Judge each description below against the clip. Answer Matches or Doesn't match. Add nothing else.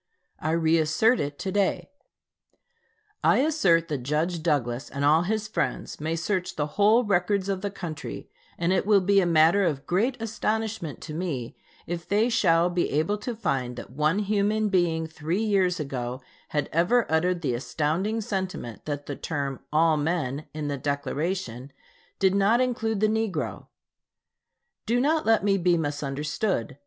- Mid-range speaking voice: Matches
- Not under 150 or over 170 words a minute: Matches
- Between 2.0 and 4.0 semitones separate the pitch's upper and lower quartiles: Doesn't match